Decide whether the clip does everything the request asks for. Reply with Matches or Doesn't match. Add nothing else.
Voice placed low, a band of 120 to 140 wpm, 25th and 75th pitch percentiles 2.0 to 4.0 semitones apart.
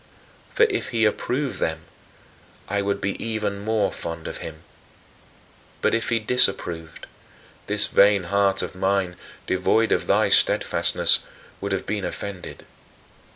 Matches